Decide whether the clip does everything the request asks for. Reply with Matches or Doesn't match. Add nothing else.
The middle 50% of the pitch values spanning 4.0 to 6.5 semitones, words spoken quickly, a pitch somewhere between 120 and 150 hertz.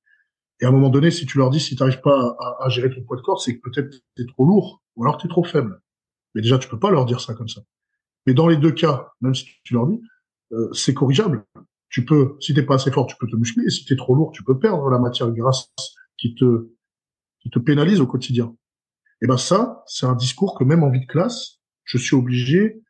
Matches